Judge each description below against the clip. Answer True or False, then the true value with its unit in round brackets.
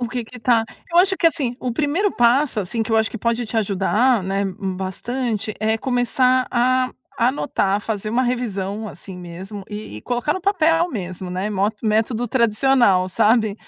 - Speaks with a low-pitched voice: False (230 Hz)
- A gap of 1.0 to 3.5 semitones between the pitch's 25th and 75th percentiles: False (4.0 semitones)